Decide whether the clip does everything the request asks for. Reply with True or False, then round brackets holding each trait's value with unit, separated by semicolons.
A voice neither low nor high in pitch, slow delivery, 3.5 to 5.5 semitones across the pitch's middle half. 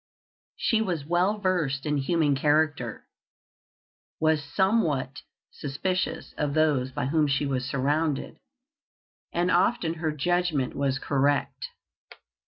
True (150 Hz; 110 wpm; 3.9 semitones)